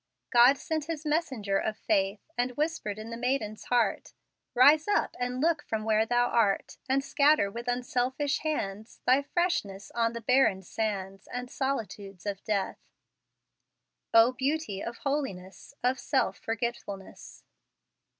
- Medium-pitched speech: No, high, 240 Hz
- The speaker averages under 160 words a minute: Yes, average, 140 wpm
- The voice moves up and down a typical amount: Yes, average, 4.7 semitones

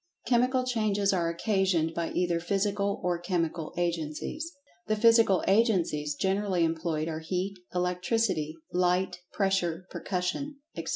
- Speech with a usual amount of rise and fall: Yes, average, 3.4 semitones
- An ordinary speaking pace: No, slow, 120 wpm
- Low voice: No, medium, 180 Hz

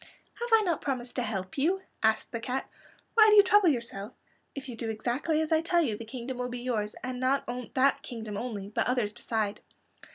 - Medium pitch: No, very high, 250 Hz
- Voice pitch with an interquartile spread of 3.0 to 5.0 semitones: No, wide, 5.4 semitones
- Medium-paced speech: No, fast, 215 wpm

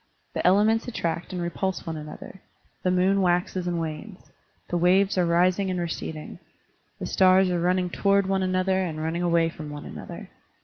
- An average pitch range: No, narrow, 2.0 semitones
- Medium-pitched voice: Yes, medium, 180 Hz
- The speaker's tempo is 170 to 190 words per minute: Yes, average, 175 wpm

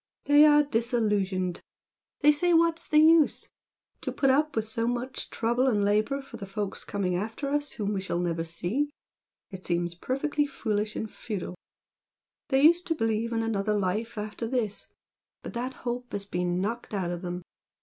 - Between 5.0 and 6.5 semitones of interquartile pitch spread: Yes, wide, 5.6 semitones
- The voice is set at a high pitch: Yes, high, 225 Hz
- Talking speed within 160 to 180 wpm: Yes, average, 175 wpm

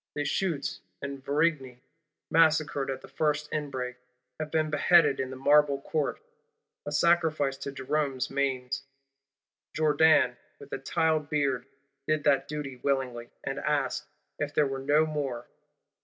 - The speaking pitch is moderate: Yes, medium, 145 Hz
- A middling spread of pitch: No, narrow, 2.2 semitones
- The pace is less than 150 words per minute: Yes, slow, 135 wpm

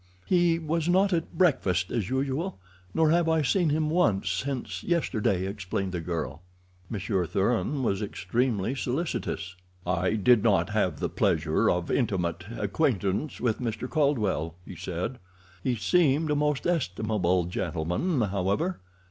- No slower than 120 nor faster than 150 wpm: Yes, average, 140 wpm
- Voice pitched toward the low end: Yes, low, 110 Hz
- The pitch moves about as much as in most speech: No, wide, 8.5 semitones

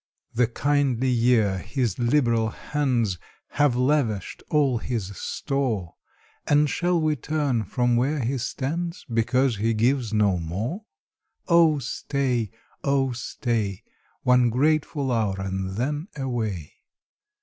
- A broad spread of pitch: No, average, 4.4 semitones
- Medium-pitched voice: No, low, 125 Hz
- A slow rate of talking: Yes, slow, 115 wpm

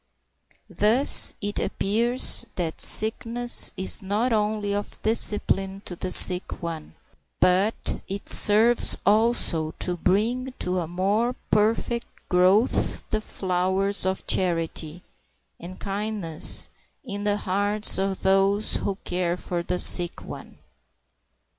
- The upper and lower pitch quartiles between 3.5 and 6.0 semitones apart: No, average, 2.9 semitones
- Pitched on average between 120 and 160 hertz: No, high, 200 Hz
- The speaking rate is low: Yes, slow, 115 wpm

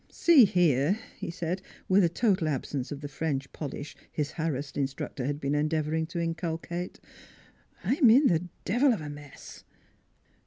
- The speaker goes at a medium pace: Yes, average, 165 wpm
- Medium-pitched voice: Yes, medium, 160 Hz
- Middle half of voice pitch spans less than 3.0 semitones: No, average, 3.7 semitones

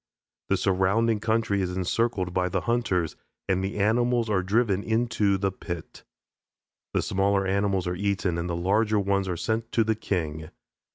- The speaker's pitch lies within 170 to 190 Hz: No, low, 100 Hz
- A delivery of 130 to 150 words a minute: No, average, 165 wpm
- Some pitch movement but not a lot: Yes, average, 3.3 semitones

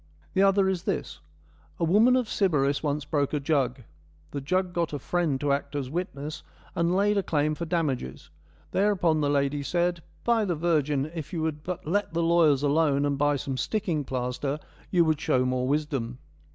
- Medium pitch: Yes, medium, 155 Hz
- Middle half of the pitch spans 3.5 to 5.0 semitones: Yes, average, 3.9 semitones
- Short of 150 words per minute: No, average, 190 wpm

